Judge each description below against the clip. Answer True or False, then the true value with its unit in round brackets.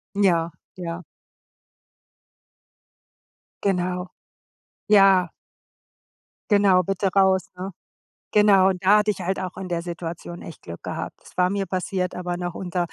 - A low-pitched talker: False (185 Hz)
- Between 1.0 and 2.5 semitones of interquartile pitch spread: True (1.8 semitones)